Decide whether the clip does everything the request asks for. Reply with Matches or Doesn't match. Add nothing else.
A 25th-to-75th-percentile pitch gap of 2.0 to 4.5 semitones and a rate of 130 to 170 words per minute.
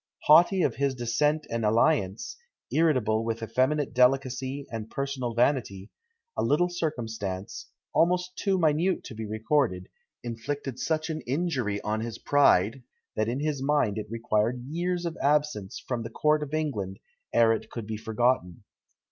Doesn't match